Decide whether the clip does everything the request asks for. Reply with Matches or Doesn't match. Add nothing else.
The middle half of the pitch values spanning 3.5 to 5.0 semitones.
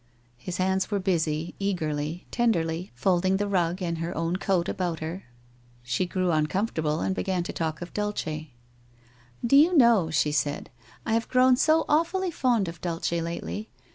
Matches